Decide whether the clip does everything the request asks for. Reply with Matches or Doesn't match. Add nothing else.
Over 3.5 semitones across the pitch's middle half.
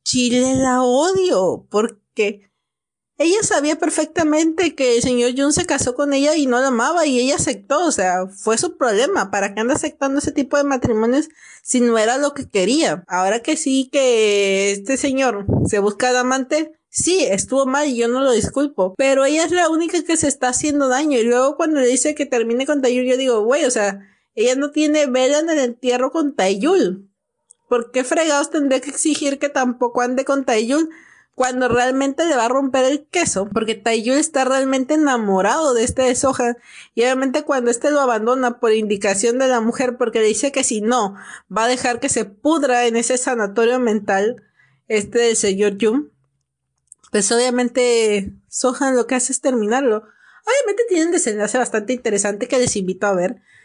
Matches